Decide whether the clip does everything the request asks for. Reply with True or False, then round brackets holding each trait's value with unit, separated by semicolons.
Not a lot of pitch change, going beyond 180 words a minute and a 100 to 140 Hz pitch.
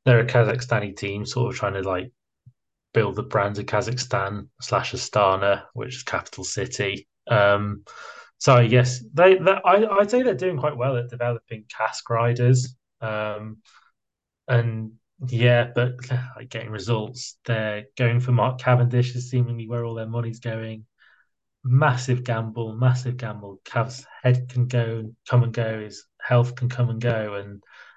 False (2.3 semitones; 155 wpm; 120 Hz)